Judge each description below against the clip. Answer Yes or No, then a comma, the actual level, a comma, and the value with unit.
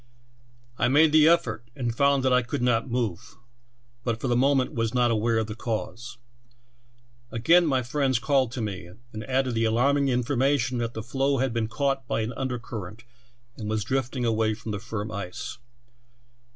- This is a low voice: Yes, low, 120 Hz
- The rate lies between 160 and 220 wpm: Yes, average, 180 wpm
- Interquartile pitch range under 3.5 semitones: Yes, average, 3.1 semitones